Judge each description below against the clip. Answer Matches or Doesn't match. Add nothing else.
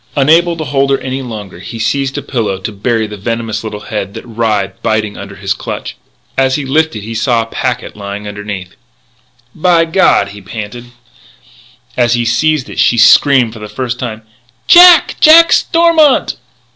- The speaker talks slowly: Doesn't match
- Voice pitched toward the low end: Matches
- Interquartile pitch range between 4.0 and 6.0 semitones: Matches